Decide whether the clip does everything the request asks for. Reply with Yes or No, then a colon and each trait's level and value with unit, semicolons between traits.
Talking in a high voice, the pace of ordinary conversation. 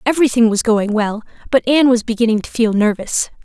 Yes: high, 230 Hz; average, 190 wpm